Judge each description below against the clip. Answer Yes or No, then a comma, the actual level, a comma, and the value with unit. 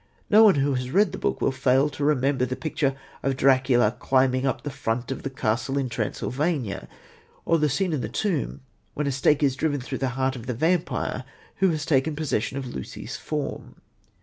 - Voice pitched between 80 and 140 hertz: Yes, low, 135 Hz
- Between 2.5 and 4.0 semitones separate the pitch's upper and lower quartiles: Yes, average, 2.8 semitones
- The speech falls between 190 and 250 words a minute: Yes, average, 200 wpm